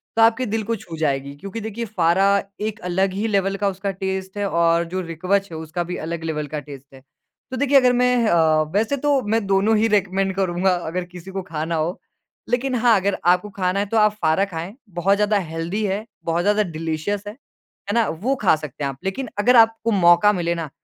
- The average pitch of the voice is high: Yes, high, 195 Hz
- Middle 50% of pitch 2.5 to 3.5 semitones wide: No, average, 4.1 semitones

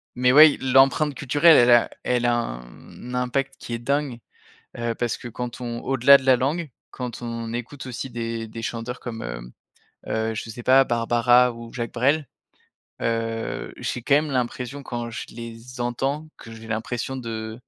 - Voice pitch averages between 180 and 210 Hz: No, low, 120 Hz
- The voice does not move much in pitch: Yes, narrow, 2.3 semitones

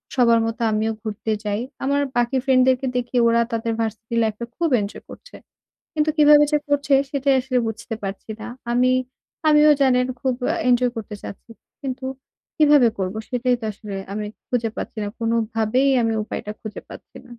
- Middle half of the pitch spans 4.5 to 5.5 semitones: No, average, 3.2 semitones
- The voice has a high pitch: Yes, high, 240 Hz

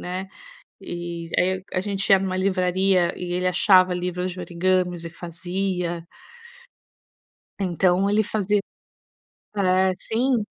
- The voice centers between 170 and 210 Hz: Yes, medium, 185 Hz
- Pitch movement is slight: Yes, narrow, 1.5 semitones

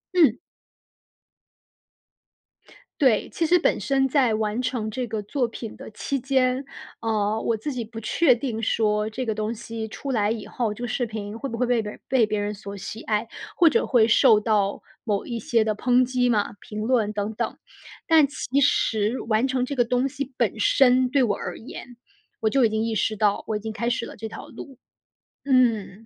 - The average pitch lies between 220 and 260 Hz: Yes, high, 230 Hz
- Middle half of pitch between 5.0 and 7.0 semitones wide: No, average, 2.9 semitones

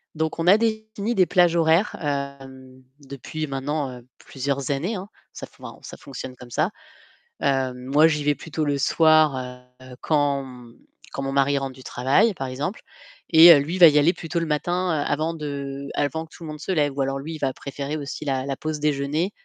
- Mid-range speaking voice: Yes, medium, 145 Hz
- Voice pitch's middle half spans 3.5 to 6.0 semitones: No, average, 3.0 semitones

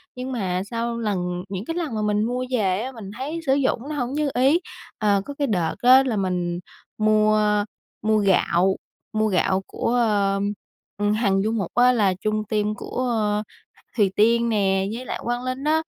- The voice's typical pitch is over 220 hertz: No, high, 215 Hz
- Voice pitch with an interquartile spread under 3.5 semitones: No, average, 4.1 semitones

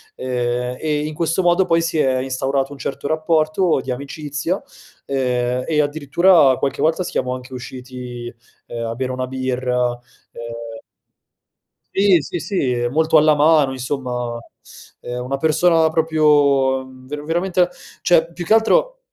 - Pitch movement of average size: Yes, average, 4.1 semitones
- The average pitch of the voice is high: No, medium, 140 Hz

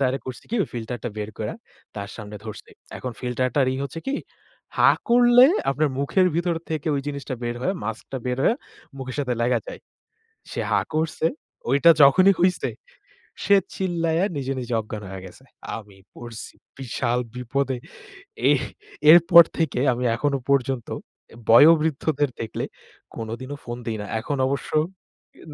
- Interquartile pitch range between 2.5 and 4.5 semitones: No, average, 5.1 semitones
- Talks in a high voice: No, low, 135 Hz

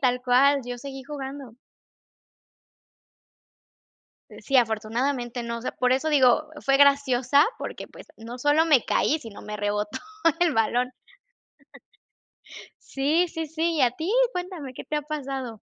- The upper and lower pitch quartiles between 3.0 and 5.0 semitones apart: Yes, average, 3.3 semitones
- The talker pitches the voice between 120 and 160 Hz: No, very high, 270 Hz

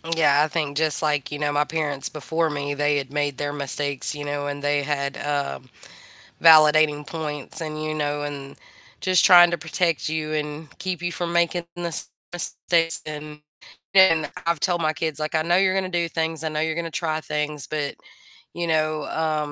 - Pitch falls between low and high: Yes, medium, 155 Hz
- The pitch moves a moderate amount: No, narrow, 2.0 semitones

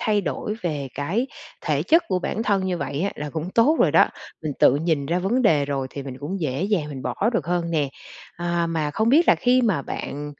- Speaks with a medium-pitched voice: Yes, medium, 170 Hz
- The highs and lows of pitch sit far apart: Yes, wide, 5.8 semitones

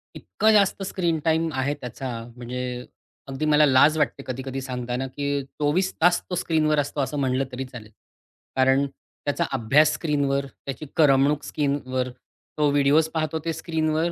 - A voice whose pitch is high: No, medium, 145 Hz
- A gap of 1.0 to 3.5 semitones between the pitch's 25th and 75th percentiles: Yes, average, 3.0 semitones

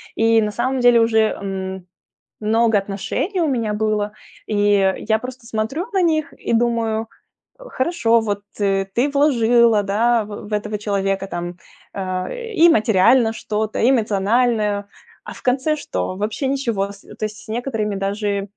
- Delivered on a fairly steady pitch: No, average, 3.2 semitones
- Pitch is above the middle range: Yes, high, 220 Hz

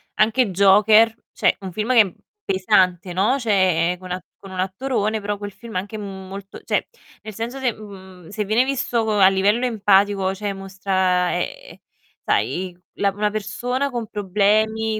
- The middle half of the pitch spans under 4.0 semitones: Yes, narrow, 2.6 semitones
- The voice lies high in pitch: Yes, high, 205 Hz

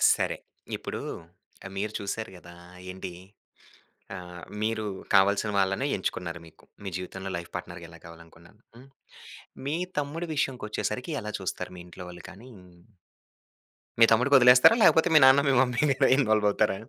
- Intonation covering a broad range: Yes, wide, 5.7 semitones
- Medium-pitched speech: No, low, 105 Hz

